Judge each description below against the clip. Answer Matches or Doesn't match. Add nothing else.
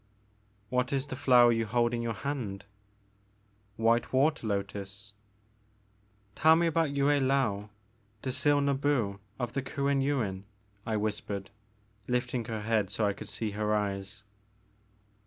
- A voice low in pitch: Matches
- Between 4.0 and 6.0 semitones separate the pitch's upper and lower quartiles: Matches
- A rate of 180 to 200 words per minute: Doesn't match